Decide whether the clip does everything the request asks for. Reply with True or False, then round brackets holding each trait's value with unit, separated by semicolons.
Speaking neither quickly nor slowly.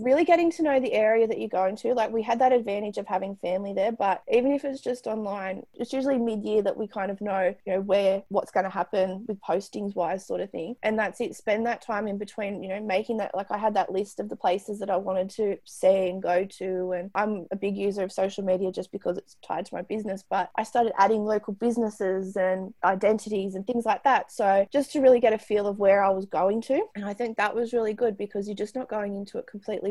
False (260 wpm)